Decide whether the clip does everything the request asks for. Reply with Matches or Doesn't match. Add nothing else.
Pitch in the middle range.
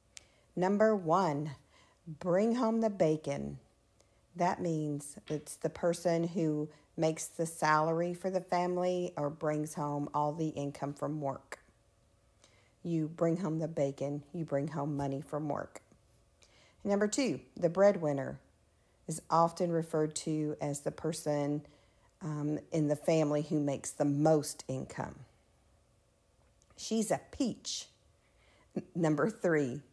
Matches